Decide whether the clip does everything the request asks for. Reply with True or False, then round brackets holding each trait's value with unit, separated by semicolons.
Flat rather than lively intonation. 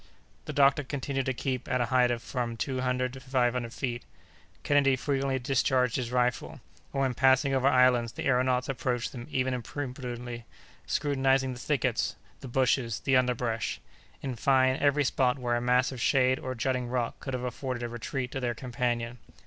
True (1.5 semitones)